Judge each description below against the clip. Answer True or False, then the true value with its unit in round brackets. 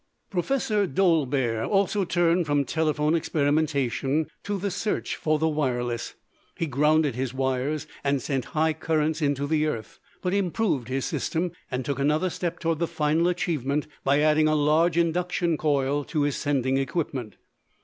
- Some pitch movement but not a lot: True (3.4 semitones)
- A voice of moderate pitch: True (155 Hz)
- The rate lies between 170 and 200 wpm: False (155 wpm)